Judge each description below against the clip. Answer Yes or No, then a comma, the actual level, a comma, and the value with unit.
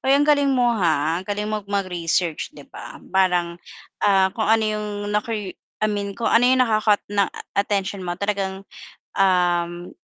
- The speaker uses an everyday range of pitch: Yes, average, 3.1 semitones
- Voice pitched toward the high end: Yes, high, 200 Hz